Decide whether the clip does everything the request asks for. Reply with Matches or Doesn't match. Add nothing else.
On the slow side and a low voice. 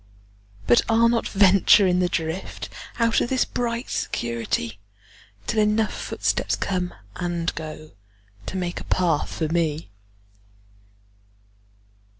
Doesn't match